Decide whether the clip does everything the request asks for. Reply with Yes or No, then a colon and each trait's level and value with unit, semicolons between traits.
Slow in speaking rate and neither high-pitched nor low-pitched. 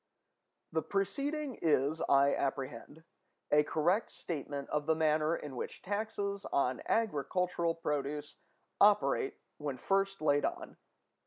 Yes: slow, 115 wpm; medium, 155 Hz